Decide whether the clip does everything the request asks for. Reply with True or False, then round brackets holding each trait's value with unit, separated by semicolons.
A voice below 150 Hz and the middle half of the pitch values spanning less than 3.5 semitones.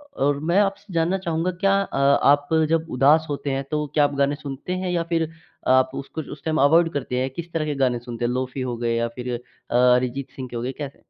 False (140 Hz; 4.1 semitones)